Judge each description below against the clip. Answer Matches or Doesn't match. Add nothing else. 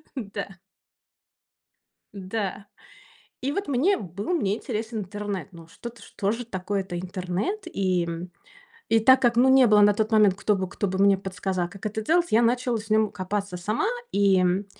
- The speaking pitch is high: Matches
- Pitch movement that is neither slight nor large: Matches